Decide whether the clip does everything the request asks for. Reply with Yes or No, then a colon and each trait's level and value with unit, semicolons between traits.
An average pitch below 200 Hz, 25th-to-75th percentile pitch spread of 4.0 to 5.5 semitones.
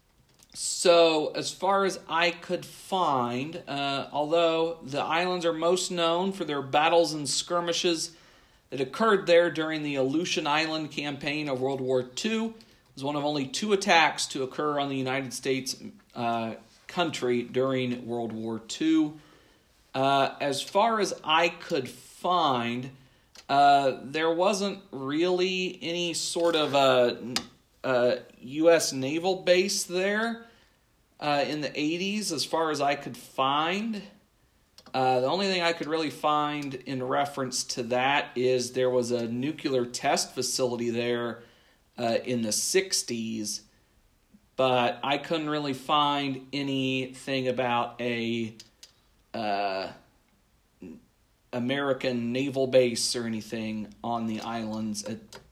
Yes: medium, 140 Hz; average, 5.0 semitones